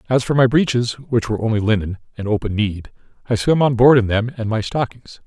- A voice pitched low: Yes, low, 115 Hz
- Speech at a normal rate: No, fast, 230 wpm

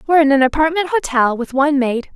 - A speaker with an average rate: No, fast, 220 wpm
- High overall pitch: Yes, very high, 285 Hz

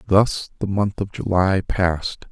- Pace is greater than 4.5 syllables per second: No, 4.1 syllables/s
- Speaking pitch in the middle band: No, very low, 95 Hz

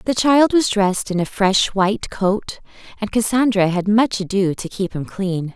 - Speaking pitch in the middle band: No, high, 205 Hz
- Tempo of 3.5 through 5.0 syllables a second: Yes, 4.5 syllables/s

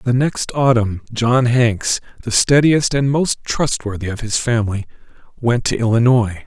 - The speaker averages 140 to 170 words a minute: Yes, average, 150 wpm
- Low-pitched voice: Yes, low, 120 Hz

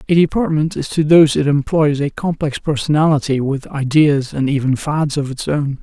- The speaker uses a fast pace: No, average, 185 wpm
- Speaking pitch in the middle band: Yes, medium, 145 Hz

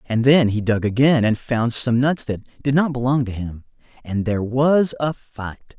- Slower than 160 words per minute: No, fast, 205 wpm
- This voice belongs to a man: Yes, male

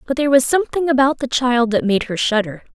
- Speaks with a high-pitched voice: Yes, very high, 255 Hz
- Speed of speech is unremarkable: No, fast, 240 wpm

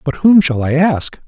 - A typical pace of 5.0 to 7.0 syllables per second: No, 4.4 syllables/s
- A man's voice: Yes, male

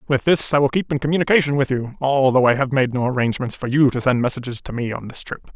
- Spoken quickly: Yes, fast, 270 wpm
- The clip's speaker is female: No, male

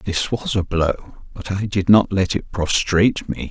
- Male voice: Yes, male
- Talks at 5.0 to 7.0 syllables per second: No, 4.1 syllables/s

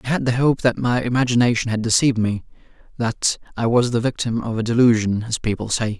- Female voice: No, male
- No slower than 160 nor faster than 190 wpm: No, average, 200 wpm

